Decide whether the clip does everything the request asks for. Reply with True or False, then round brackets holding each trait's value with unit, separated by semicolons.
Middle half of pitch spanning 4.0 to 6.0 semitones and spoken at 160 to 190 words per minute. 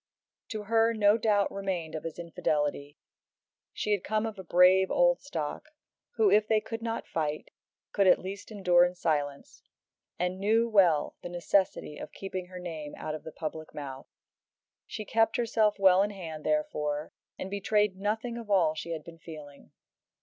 True (5.0 semitones; 170 wpm)